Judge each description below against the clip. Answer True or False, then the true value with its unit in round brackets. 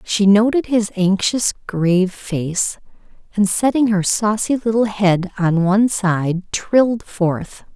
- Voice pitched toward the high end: True (200 Hz)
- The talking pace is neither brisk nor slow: False (130 wpm)